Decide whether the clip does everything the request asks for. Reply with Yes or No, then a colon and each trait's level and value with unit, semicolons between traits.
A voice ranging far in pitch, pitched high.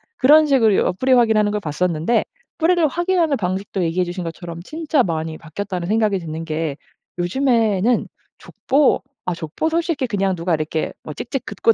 Yes: wide, 7.6 semitones; high, 200 Hz